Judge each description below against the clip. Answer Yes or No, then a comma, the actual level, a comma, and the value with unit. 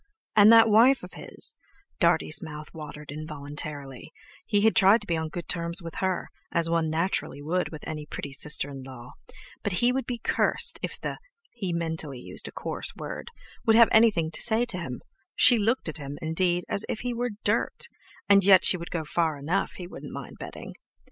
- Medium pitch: Yes, medium, 170 Hz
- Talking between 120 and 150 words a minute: No, average, 190 wpm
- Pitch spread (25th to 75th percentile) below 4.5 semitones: No, wide, 5.5 semitones